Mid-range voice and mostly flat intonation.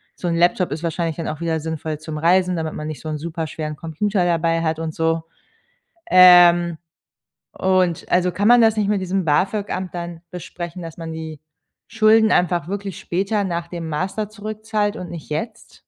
No: medium, 175 Hz; average, 3.0 semitones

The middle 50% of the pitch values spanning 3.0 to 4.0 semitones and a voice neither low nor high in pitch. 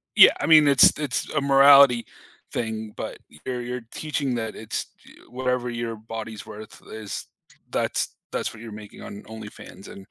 No: average, 3.6 semitones; low, 120 Hz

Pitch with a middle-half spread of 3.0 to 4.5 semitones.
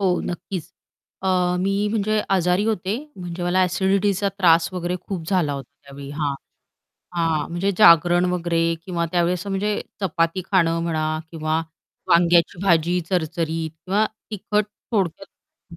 No: narrow, 2.6 semitones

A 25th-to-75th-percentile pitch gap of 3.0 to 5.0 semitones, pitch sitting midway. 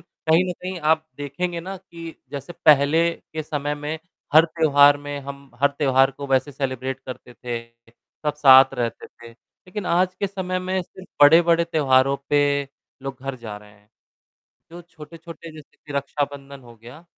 Yes: average, 3.9 semitones; medium, 145 Hz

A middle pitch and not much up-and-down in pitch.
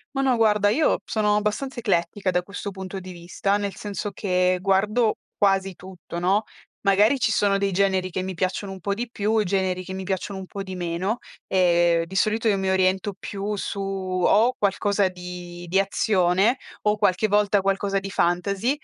No: high, 195 Hz; narrow, 2.0 semitones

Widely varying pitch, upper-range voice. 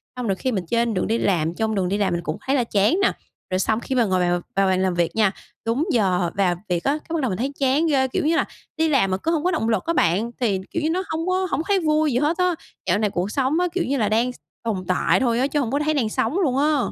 Yes: wide, 7.7 semitones; high, 235 Hz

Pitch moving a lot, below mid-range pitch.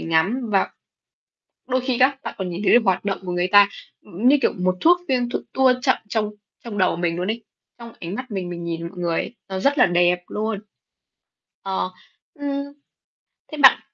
No: wide, 5.8 semitones; high, 200 Hz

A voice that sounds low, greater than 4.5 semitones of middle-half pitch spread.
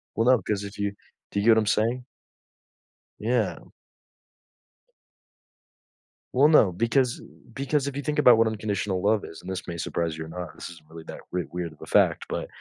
Yes: low, 105 Hz; wide, 5.4 semitones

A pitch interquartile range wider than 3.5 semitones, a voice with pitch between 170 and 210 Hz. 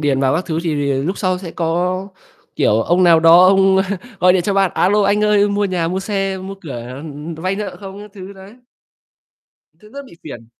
No: average, 3.2 semitones; medium, 185 Hz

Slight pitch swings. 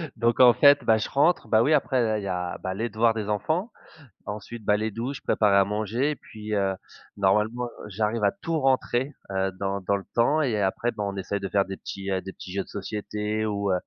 No: average, 3.3 semitones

